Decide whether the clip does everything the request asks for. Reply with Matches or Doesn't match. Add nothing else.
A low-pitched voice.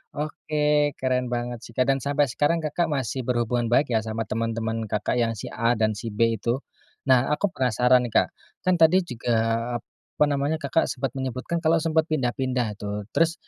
Matches